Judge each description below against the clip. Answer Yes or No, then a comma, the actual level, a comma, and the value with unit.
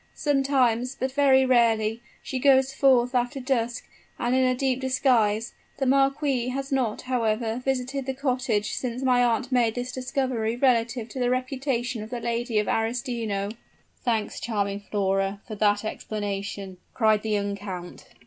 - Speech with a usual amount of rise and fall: Yes, average, 3.2 semitones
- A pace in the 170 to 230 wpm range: No, average, 155 wpm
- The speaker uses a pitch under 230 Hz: No, high, 245 Hz